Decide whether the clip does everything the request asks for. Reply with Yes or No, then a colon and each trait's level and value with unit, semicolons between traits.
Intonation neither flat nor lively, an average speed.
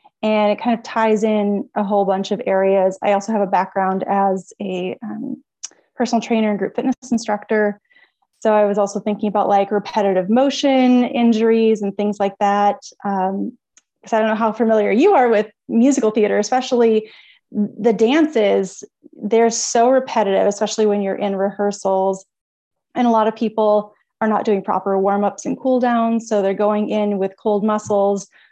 No: narrow, 2.2 semitones; average, 170 wpm